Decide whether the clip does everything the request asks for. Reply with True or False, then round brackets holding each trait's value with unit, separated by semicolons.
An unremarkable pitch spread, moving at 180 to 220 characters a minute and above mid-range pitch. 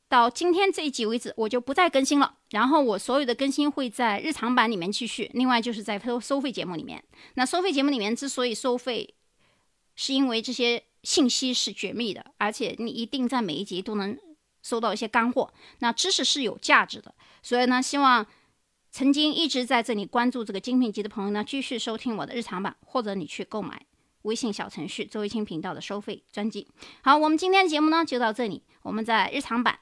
False (3.8 semitones; 330 characters per minute; 240 Hz)